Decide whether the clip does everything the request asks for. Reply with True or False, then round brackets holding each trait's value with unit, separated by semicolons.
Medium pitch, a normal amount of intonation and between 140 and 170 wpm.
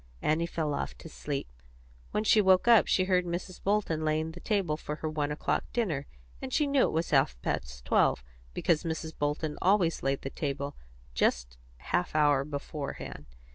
False (155 Hz; 4.1 semitones; 180 wpm)